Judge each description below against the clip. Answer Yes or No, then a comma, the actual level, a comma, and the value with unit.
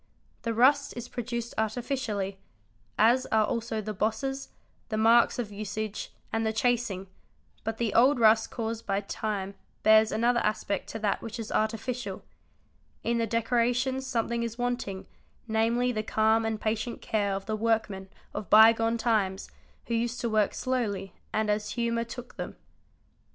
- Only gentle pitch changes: Yes, narrow, 1.8 semitones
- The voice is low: No, high, 225 Hz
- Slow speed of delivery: No, average, 155 wpm